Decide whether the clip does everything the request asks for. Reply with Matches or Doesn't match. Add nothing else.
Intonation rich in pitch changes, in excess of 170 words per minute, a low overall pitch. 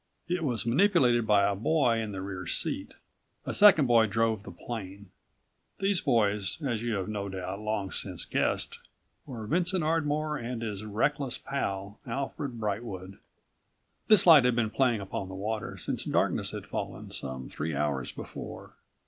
Doesn't match